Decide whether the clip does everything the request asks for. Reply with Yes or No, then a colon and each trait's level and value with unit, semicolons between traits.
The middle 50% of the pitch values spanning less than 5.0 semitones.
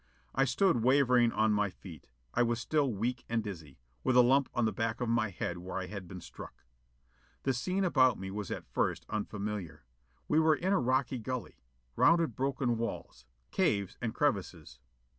Yes: average, 4.6 semitones